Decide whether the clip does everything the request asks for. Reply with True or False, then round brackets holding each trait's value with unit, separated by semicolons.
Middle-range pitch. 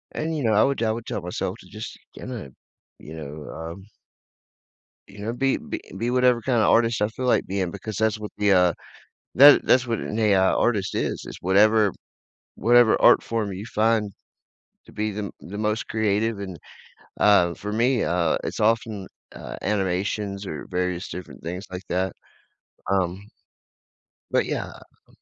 False (105 Hz)